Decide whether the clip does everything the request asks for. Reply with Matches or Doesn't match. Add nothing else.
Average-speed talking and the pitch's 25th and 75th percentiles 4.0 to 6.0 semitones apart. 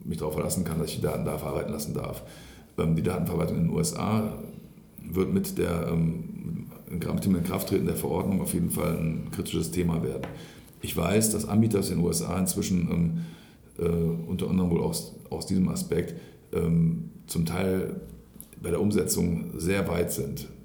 Matches